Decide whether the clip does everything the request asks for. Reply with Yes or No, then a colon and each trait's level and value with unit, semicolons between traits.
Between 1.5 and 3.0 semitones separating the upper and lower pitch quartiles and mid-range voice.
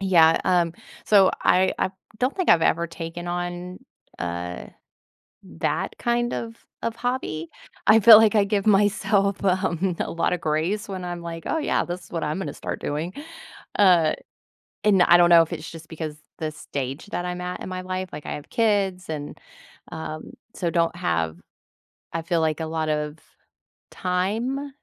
No: average, 3.6 semitones; medium, 175 Hz